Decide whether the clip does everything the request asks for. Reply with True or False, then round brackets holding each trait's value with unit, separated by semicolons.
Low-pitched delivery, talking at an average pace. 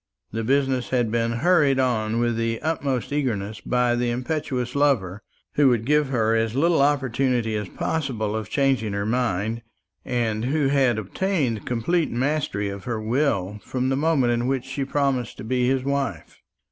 True (125 Hz; 170 wpm)